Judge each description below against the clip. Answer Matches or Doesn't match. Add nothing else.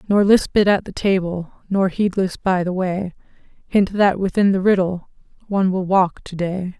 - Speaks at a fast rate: Doesn't match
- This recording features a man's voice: Doesn't match